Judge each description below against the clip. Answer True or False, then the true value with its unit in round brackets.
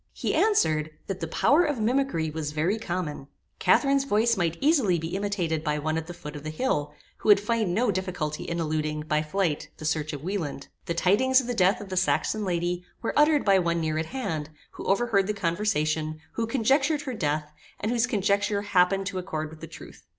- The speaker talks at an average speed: False (210 wpm)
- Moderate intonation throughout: False (5.7 semitones)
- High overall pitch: False (180 Hz)